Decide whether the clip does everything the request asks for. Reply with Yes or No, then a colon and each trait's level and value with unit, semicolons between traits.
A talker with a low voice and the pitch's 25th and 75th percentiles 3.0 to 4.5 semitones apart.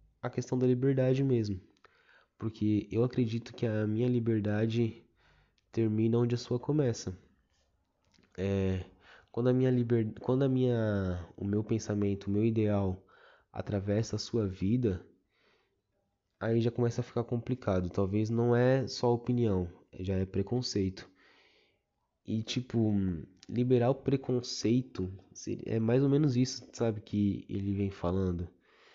Yes: low, 110 Hz; average, 3.8 semitones